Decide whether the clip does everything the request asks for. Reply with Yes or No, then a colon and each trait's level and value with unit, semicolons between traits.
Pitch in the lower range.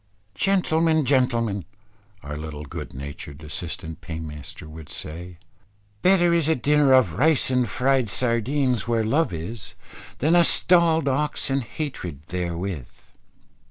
Yes: low, 120 Hz